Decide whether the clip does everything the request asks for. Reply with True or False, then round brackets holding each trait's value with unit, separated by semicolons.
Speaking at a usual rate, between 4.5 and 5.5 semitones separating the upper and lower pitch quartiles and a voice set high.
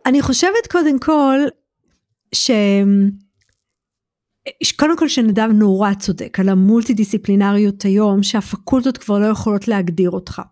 True (110 wpm; 5.0 semitones; 210 Hz)